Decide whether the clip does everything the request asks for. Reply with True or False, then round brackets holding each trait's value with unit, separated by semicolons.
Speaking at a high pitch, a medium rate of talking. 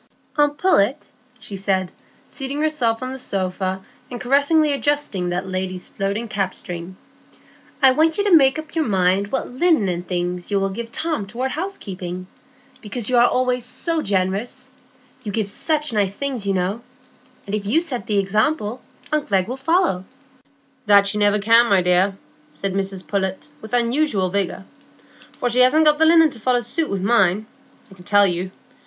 True (215 Hz; 175 wpm)